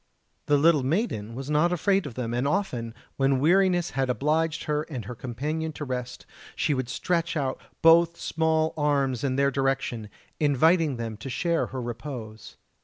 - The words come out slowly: No, average, 170 wpm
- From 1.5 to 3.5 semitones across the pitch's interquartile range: No, average, 4.3 semitones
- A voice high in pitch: No, medium, 140 Hz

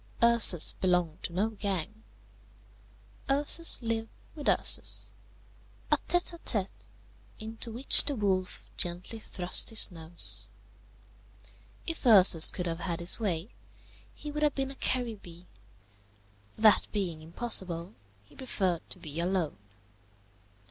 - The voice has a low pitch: No, high, 195 Hz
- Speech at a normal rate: No, slow, 120 wpm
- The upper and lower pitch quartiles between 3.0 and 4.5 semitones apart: No, average, 5.2 semitones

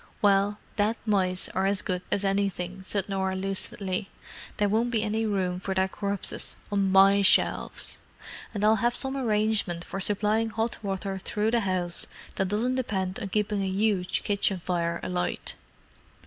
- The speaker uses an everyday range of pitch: No, narrow, 2.1 semitones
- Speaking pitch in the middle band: No, high, 200 Hz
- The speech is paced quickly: No, average, 160 wpm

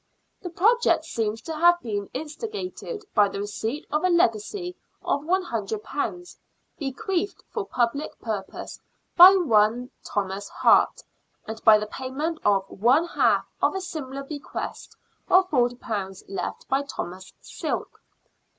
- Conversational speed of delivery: No, slow, 130 wpm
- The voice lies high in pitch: Yes, very high, 270 Hz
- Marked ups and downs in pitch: Yes, wide, 8.4 semitones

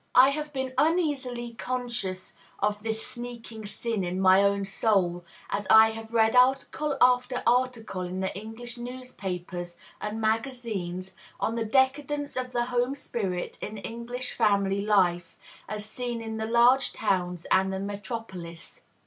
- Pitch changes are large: No, average, 4.2 semitones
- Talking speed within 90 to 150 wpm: Yes, average, 145 wpm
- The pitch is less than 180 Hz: No, high, 225 Hz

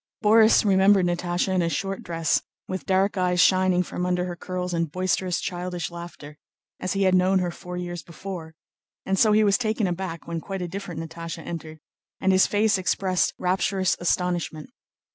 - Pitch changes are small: Yes, narrow, 1.8 semitones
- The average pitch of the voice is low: No, medium, 180 Hz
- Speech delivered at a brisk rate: No, average, 180 wpm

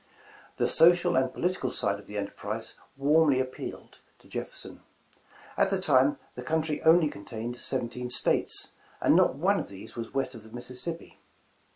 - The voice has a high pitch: No, low, 130 Hz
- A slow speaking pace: No, average, 160 wpm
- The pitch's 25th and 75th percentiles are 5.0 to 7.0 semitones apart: Yes, wide, 5.6 semitones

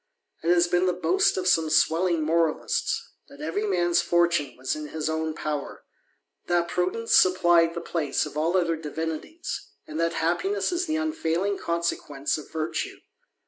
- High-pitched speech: No, medium, 170 Hz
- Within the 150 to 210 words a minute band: Yes, average, 170 wpm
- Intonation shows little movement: Yes, narrow, 2.3 semitones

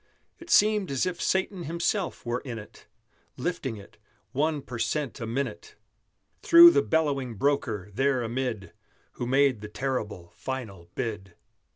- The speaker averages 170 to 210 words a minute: No, average, 145 wpm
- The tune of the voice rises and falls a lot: Yes, wide, 6.1 semitones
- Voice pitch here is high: No, low, 130 Hz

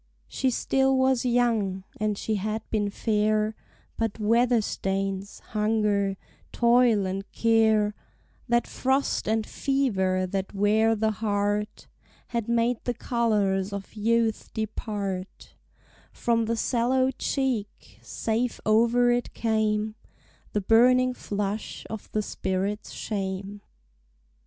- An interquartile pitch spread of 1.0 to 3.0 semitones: Yes, narrow, 2.6 semitones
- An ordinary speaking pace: No, slow, 115 wpm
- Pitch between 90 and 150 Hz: No, high, 220 Hz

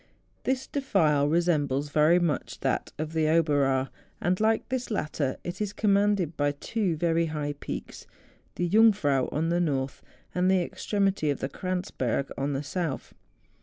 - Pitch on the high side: No, medium, 165 Hz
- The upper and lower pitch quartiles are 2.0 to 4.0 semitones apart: No, average, 4.8 semitones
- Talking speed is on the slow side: No, average, 155 wpm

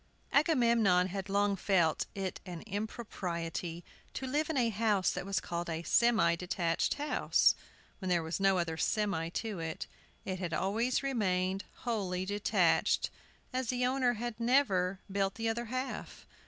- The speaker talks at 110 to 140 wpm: No, average, 155 wpm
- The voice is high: Yes, high, 195 Hz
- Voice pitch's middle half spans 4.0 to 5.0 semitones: Yes, average, 4.7 semitones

